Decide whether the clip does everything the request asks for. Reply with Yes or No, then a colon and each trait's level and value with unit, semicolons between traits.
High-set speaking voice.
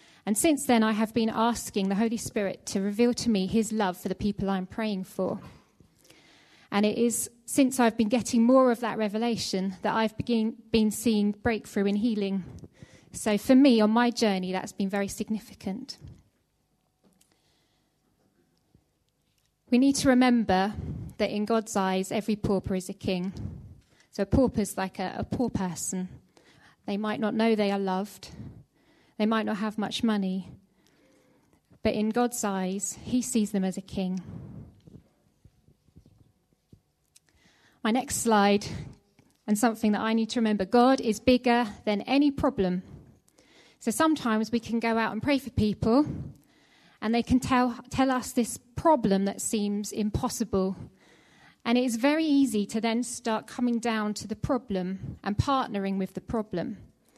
Yes: high, 220 Hz